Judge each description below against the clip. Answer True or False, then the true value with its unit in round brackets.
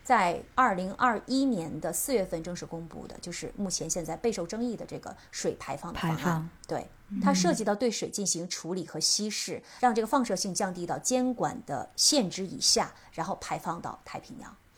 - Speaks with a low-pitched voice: False (190 Hz)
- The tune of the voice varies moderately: False (6.1 semitones)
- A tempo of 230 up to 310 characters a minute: True (290 characters per minute)